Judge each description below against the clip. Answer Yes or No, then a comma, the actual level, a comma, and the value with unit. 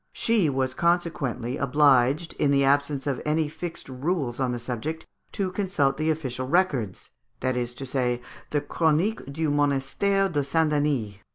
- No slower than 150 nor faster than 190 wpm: Yes, average, 160 wpm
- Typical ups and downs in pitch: Yes, average, 3.8 semitones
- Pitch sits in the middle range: Yes, medium, 145 Hz